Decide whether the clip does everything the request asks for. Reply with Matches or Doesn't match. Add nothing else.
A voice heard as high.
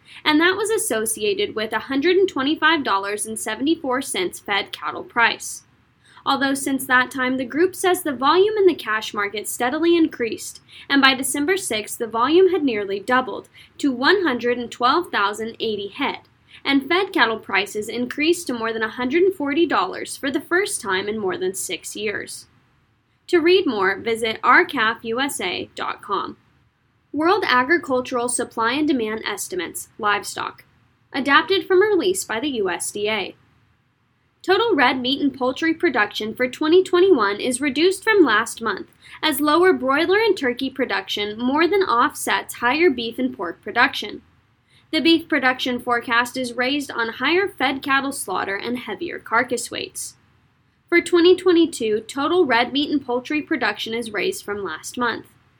Matches